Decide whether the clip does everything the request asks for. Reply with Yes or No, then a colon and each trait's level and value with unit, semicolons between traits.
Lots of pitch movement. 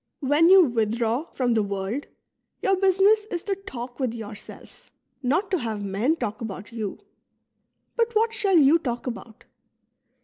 Yes: wide, 8.8 semitones